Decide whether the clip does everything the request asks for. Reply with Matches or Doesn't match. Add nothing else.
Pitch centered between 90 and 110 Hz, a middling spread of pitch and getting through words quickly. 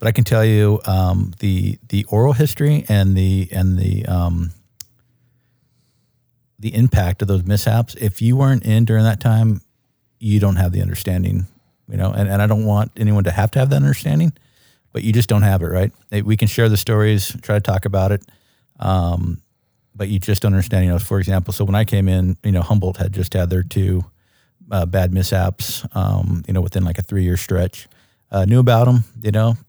Matches